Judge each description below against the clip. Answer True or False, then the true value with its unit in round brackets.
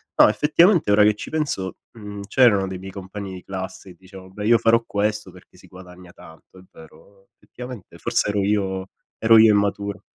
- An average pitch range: False (2.1 semitones)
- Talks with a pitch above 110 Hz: False (100 Hz)